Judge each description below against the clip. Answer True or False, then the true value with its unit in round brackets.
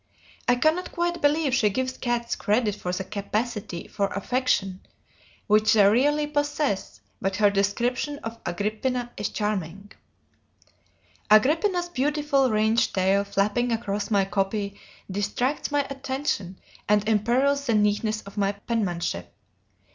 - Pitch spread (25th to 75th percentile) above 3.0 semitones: True (4.7 semitones)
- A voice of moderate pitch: False (215 Hz)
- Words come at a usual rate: False (125 wpm)